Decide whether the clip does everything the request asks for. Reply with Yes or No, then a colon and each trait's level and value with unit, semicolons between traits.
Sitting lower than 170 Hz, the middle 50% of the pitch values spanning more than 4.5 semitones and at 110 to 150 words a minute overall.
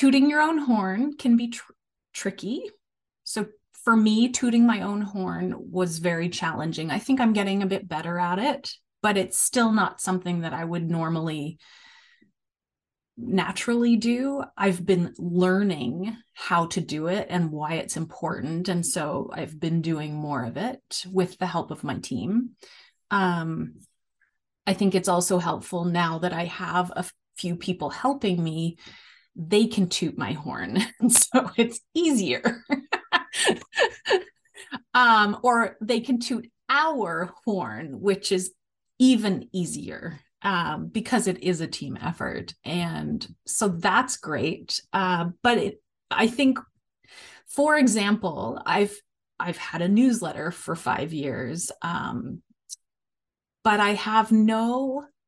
No: high, 195 Hz; average, 5.3 semitones; average, 140 wpm